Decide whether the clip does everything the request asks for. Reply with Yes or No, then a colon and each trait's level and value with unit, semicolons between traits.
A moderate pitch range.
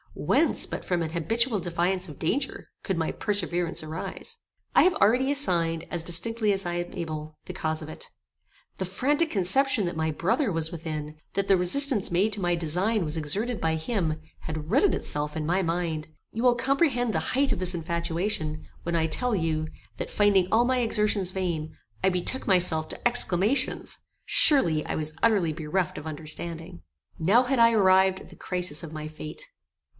Yes: average, 5.0 semitones